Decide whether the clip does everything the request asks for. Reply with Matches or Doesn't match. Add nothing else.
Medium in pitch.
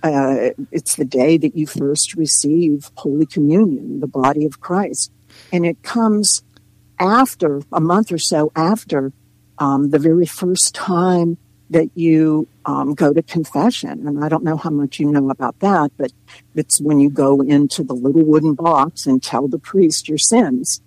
Matches